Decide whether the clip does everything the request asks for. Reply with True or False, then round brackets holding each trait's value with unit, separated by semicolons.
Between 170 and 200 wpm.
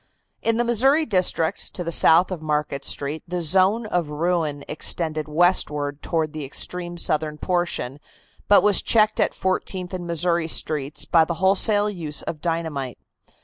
False (155 wpm)